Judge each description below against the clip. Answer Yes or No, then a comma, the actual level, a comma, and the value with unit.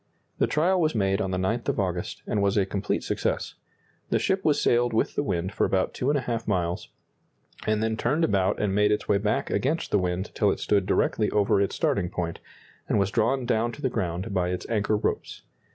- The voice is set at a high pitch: No, low, 105 Hz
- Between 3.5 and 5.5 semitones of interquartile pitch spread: Yes, average, 3.8 semitones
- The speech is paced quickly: Yes, fast, 215 wpm